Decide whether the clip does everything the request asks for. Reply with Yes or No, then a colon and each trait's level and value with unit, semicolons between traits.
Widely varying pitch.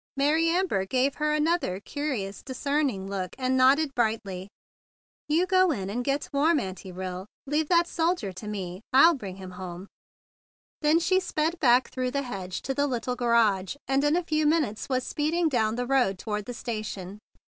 Yes: wide, 7.3 semitones